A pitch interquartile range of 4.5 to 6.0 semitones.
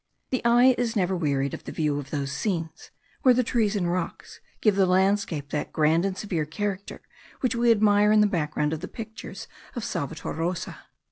Yes: average, 5.2 semitones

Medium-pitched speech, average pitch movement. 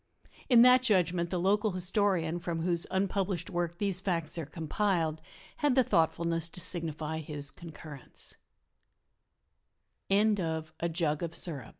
Yes: medium, 175 Hz; average, 3.1 semitones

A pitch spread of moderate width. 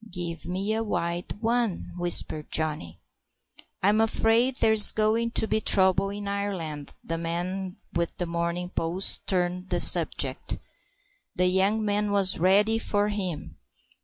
Yes: average, 3.5 semitones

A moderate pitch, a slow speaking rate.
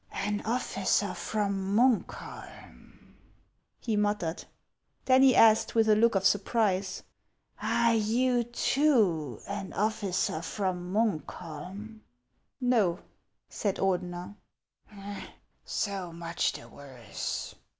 No: high, 205 Hz; slow, 105 wpm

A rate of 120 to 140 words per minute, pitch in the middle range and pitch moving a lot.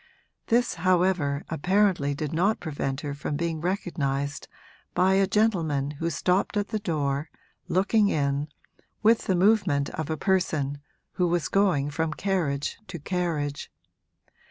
No: slow, 135 wpm; medium, 165 Hz; average, 4.9 semitones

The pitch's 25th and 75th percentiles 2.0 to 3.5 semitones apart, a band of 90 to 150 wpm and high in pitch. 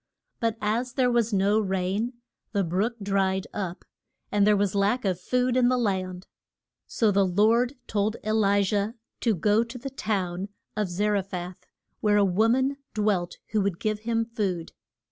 No: average, 3.0 semitones; average, 180 wpm; high, 210 Hz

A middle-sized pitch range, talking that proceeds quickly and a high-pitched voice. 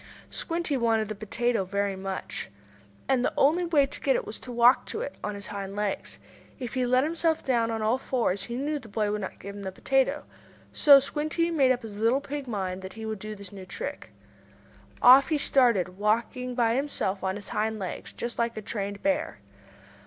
Yes: average, 5.0 semitones; fast, 210 wpm; high, 235 Hz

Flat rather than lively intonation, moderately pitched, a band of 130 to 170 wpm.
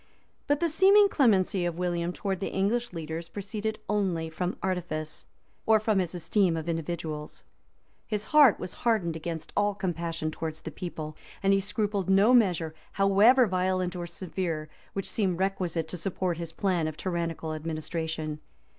No: average, 3.7 semitones; medium, 180 Hz; average, 160 wpm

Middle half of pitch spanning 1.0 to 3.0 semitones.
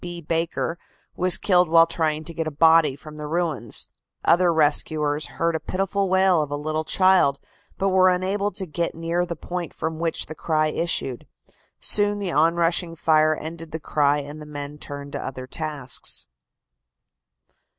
Yes: narrow, 2.6 semitones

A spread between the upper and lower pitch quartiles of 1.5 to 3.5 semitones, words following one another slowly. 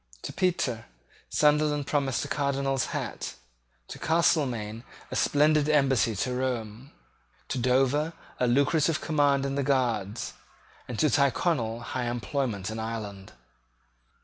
No: average, 4.0 semitones; slow, 120 wpm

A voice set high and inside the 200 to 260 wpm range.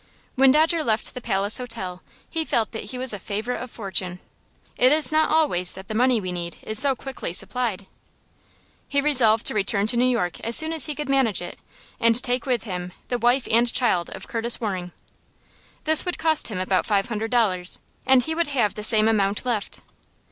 Yes: high, 230 Hz; fast, 205 wpm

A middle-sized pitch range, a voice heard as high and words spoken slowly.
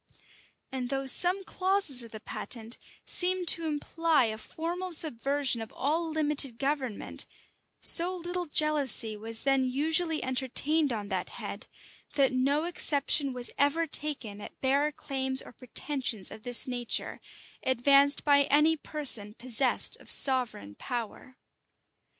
Yes: average, 4.0 semitones; very high, 275 Hz; slow, 130 wpm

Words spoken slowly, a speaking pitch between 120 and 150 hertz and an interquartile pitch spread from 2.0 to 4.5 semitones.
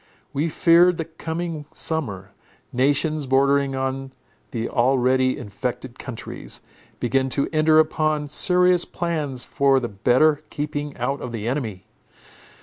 Yes: slow, 125 wpm; medium, 140 Hz; average, 3.5 semitones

